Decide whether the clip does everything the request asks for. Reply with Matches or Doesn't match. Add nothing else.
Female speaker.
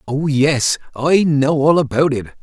Doesn't match